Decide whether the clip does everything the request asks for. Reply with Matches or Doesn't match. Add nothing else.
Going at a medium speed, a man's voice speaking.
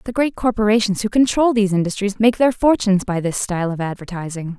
Doesn't match